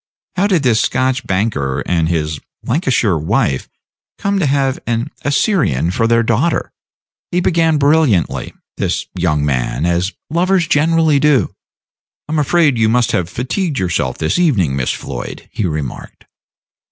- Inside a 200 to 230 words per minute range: No, average, 145 wpm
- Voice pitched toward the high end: No, low, 120 Hz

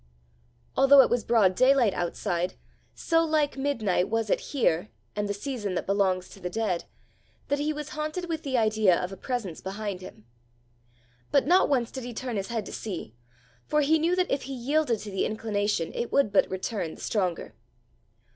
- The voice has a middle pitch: No, high, 225 Hz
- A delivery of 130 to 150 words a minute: No, average, 190 wpm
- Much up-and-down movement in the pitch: Yes, wide, 6.3 semitones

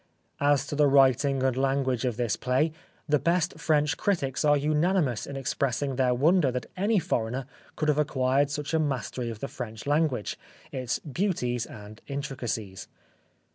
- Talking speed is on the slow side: No, average, 160 wpm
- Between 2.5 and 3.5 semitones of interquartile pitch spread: Yes, average, 3.2 semitones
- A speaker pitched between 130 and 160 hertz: Yes, low, 135 Hz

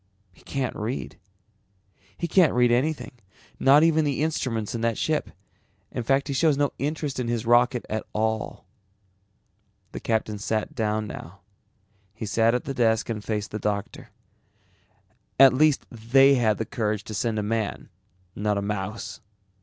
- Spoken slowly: No, average, 160 wpm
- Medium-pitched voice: No, low, 115 Hz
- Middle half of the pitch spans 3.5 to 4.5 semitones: Yes, average, 4.2 semitones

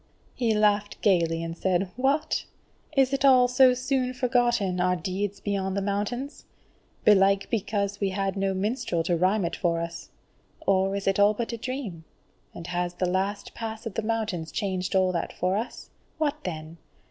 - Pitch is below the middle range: No, high, 200 Hz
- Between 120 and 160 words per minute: No, average, 175 wpm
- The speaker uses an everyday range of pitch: Yes, average, 3.9 semitones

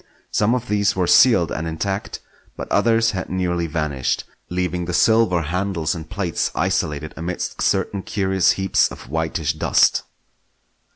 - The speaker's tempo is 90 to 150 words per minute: Yes, average, 140 wpm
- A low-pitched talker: Yes, very low, 90 Hz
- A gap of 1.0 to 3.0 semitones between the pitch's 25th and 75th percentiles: No, average, 3.6 semitones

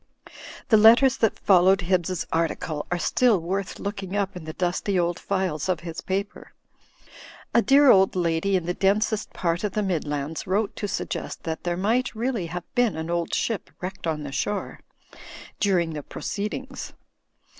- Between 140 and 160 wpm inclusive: No, average, 170 wpm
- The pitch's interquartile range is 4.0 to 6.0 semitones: No, average, 3.6 semitones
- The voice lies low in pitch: No, medium, 185 Hz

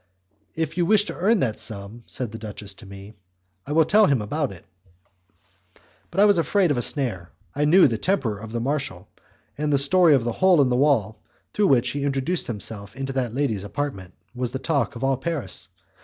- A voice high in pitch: No, low, 135 Hz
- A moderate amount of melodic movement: No, wide, 5.9 semitones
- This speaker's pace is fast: Yes, fast, 215 wpm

